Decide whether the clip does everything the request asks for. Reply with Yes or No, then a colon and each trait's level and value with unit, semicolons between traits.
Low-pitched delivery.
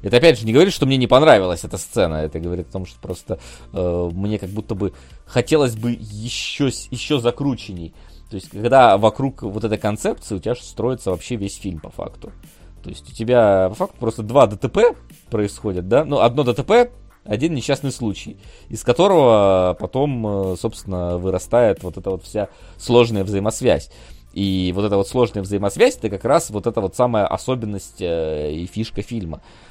Yes: low, 105 Hz